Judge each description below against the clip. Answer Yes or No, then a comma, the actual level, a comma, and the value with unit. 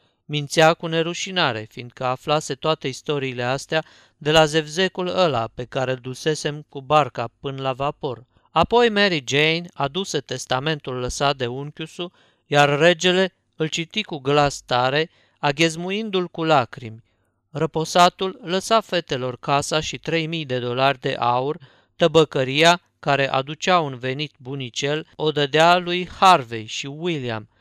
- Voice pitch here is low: No, medium, 150 Hz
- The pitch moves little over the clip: No, average, 4.2 semitones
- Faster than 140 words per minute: No, average, 135 wpm